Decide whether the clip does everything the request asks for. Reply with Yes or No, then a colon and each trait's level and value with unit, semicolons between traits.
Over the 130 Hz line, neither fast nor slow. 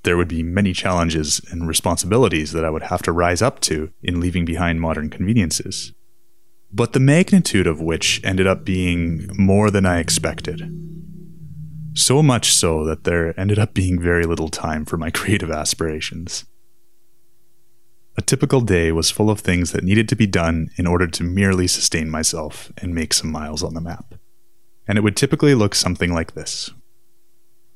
No: very low, 95 Hz; average, 175 wpm